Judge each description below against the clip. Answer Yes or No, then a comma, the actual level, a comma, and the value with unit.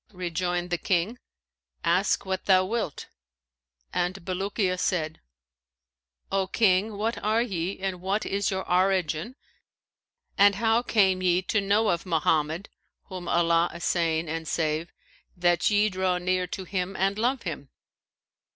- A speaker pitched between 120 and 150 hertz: No, medium, 185 Hz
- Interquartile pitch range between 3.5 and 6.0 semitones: No, narrow, 2.5 semitones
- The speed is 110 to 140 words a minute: Yes, slow, 135 wpm